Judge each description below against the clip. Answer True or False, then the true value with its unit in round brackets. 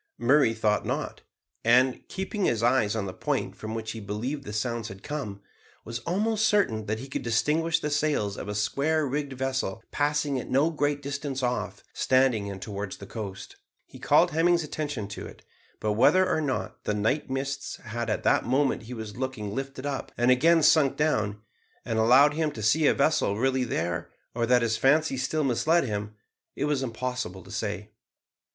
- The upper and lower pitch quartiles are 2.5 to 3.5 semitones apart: False (5.0 semitones)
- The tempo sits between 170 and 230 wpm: True (190 wpm)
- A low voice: True (130 Hz)